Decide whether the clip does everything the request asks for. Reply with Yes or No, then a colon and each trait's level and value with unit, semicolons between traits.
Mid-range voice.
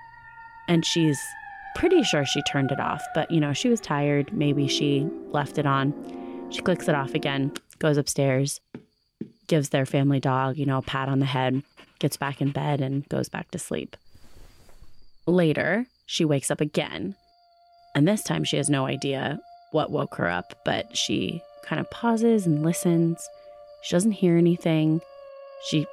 Yes: medium, 150 Hz